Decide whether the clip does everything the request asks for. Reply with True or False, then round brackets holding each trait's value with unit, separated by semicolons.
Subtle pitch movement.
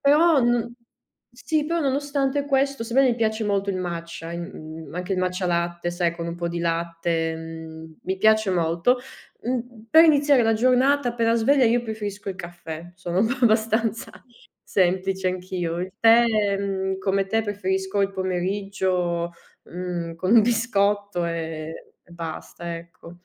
False (5.1 semitones)